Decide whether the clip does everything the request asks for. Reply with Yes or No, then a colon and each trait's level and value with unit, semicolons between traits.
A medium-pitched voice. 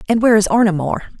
No: high, 205 Hz